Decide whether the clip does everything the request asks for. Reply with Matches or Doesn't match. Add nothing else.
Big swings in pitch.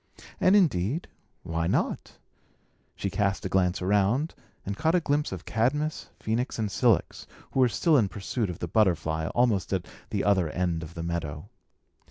Matches